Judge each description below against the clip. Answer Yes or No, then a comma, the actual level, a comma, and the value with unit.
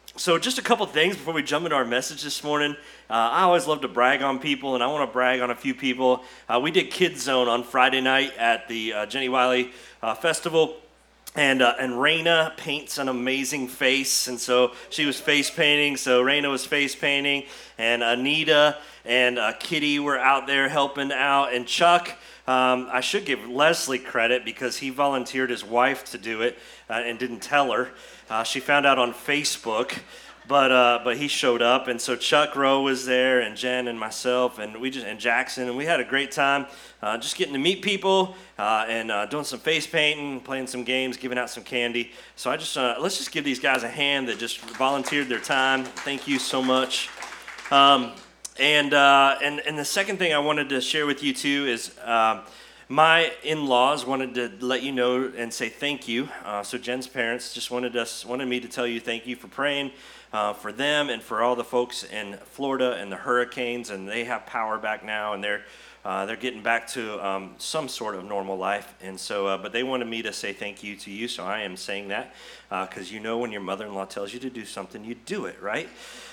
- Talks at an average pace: No, fast, 220 wpm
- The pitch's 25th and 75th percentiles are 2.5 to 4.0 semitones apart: Yes, average, 3.0 semitones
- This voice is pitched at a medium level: No, low, 130 Hz